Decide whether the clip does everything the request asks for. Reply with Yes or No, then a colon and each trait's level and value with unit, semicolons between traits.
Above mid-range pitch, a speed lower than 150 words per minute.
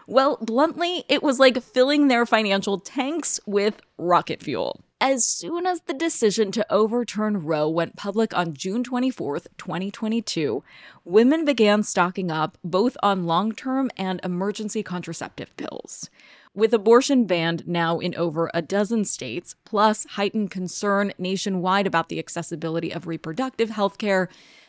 Yes: high, 205 Hz; average, 140 wpm